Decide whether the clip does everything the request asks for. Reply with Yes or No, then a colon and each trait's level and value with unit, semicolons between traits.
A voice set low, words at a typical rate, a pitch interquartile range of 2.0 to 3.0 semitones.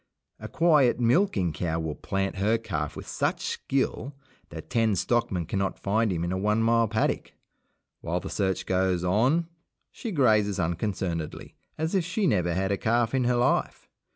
No: low, 105 Hz; average, 170 wpm; average, 4.9 semitones